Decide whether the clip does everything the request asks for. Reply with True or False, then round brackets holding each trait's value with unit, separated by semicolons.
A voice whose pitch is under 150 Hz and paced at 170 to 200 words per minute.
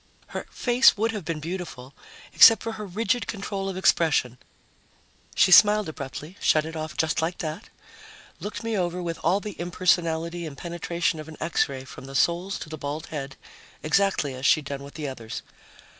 False (170 Hz; 185 wpm)